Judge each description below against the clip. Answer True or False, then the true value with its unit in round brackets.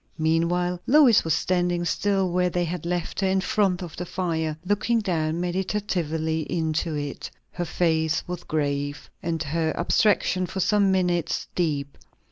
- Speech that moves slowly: False (150 wpm)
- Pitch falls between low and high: True (175 Hz)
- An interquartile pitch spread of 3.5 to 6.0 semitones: False (2.6 semitones)